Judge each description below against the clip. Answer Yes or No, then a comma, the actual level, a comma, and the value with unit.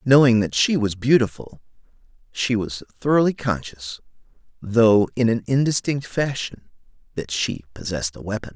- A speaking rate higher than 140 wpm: No, slow, 135 wpm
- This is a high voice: No, low, 110 Hz